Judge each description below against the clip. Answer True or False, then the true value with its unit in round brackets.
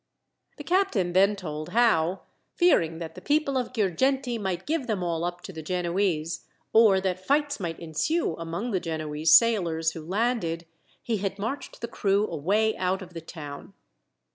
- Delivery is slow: False (165 wpm)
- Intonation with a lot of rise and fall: True (5.7 semitones)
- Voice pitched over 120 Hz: True (185 Hz)